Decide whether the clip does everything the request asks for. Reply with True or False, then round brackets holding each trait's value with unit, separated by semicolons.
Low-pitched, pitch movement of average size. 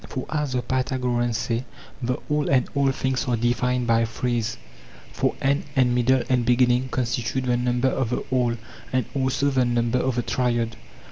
False (125 Hz; 1.5 semitones)